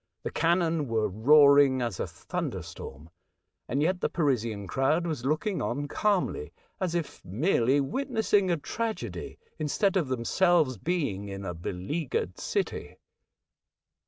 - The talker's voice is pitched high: No, medium, 145 Hz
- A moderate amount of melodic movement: No, wide, 7.0 semitones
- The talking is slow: Yes, slow, 130 wpm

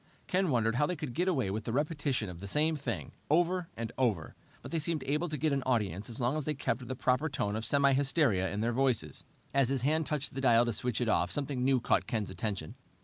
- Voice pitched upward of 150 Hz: No, low, 130 Hz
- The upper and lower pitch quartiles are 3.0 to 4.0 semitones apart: No, average, 4.7 semitones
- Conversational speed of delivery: No, fast, 250 wpm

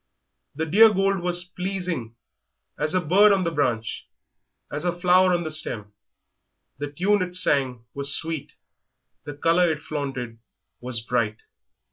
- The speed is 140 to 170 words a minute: Yes, average, 145 wpm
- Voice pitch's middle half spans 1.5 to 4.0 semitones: No, average, 4.9 semitones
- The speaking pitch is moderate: Yes, medium, 160 Hz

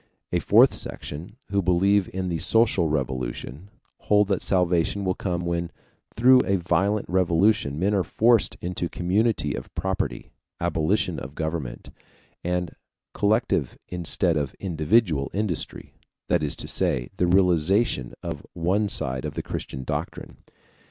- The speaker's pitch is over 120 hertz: No, very low, 90 Hz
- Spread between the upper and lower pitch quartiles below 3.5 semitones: No, average, 4.0 semitones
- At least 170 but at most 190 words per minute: No, average, 140 wpm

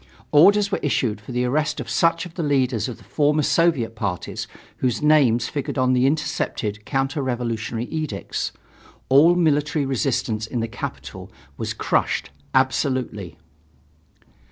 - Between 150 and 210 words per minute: No, average, 140 wpm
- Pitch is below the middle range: Yes, low, 130 Hz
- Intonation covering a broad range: No, average, 4.6 semitones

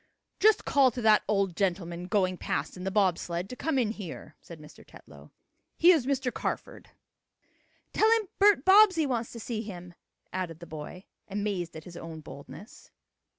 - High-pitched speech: Yes, high, 200 Hz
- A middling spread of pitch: No, wide, 6.7 semitones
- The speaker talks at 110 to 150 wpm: No, average, 175 wpm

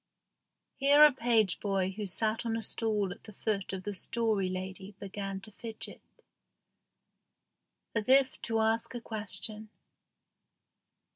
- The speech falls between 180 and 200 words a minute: No, slow, 135 wpm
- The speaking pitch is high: Yes, high, 215 Hz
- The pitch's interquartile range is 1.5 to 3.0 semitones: Yes, narrow, 2.6 semitones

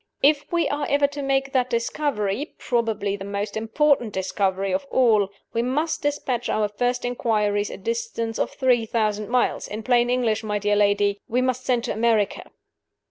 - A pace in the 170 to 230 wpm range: Yes, average, 175 wpm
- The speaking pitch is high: Yes, high, 235 Hz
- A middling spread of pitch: Yes, average, 3.9 semitones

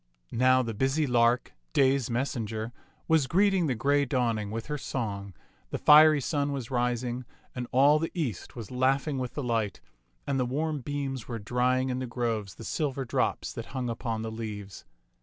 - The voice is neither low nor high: No, low, 125 Hz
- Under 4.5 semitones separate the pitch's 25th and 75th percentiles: Yes, average, 3.3 semitones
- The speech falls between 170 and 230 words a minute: Yes, average, 180 wpm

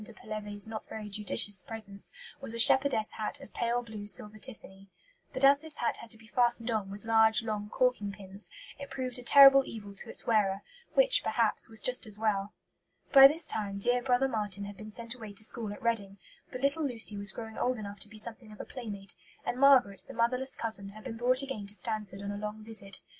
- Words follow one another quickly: Yes, fast, 220 wpm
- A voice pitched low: No, high, 220 Hz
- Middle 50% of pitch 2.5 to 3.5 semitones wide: Yes, average, 3.2 semitones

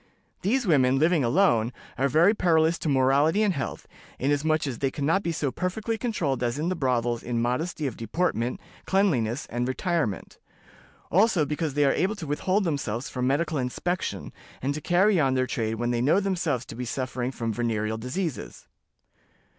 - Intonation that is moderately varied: No, wide, 6.0 semitones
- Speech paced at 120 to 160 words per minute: No, average, 180 wpm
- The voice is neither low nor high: Yes, medium, 145 Hz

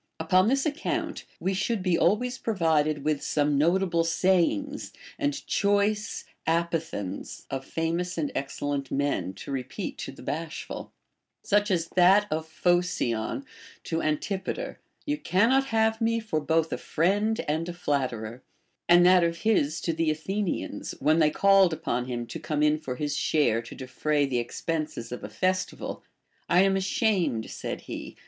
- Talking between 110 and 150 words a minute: No, average, 160 wpm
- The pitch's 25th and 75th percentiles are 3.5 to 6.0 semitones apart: Yes, average, 4.8 semitones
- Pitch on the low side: No, medium, 165 Hz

